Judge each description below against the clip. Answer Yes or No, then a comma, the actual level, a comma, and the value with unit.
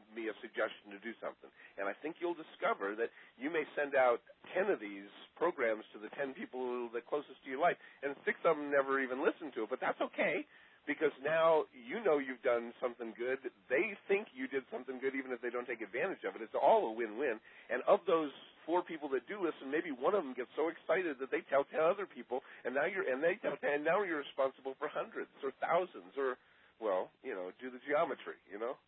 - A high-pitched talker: No, low, 135 Hz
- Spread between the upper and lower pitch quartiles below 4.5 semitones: No, average, 5.0 semitones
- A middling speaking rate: No, fast, 230 wpm